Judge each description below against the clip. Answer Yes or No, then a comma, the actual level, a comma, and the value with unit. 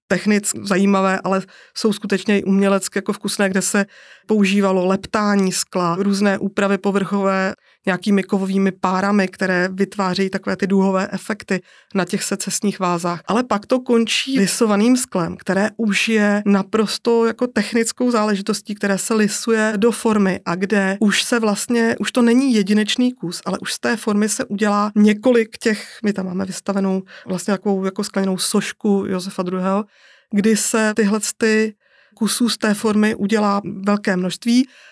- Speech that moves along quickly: No, average, 155 wpm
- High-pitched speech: Yes, high, 205 Hz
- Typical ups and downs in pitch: No, narrow, 2.2 semitones